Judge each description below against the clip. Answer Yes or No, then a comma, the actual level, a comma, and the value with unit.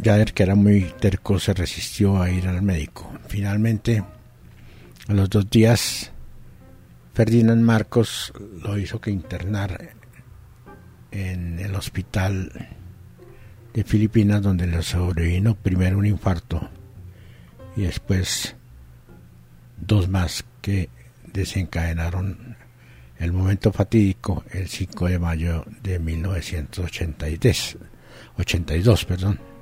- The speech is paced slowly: Yes, slow, 100 wpm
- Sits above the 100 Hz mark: No, very low, 95 Hz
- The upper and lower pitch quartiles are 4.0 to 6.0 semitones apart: No, average, 3.3 semitones